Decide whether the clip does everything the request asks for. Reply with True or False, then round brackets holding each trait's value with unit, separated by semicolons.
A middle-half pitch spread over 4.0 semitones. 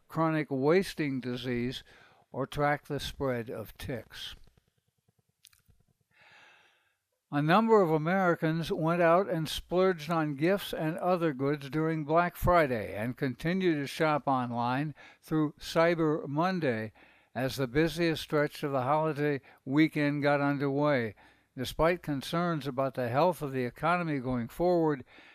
False (3.6 semitones)